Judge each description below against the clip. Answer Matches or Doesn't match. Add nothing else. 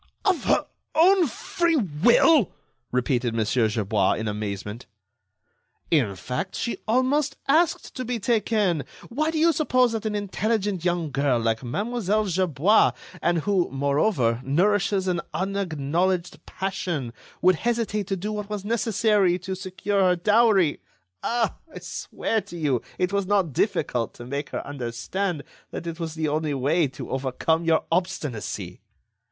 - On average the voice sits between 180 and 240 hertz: Matches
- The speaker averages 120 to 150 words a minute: Matches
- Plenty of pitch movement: Matches